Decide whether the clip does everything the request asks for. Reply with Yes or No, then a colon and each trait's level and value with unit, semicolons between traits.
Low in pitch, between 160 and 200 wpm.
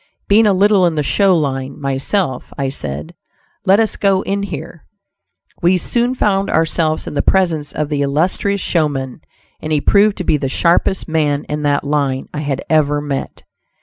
No: medium, 155 Hz; average, 180 wpm